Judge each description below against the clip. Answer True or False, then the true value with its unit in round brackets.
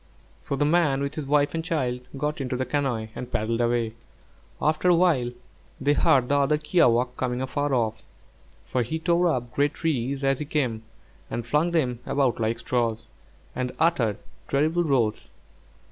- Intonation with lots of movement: False (3.8 semitones)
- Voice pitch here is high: False (135 Hz)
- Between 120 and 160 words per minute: False (170 wpm)